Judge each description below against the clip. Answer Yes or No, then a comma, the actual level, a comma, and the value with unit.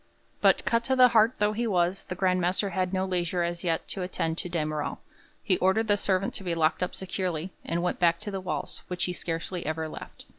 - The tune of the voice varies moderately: No, narrow, 2.3 semitones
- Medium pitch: Yes, medium, 180 Hz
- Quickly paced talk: Yes, fast, 235 wpm